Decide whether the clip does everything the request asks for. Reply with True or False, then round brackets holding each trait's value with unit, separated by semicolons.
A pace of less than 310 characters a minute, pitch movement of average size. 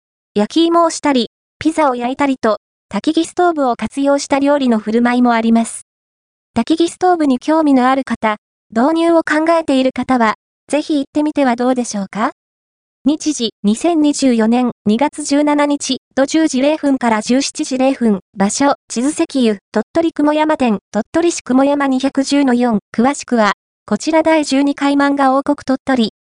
True (280 characters per minute; 4.5 semitones)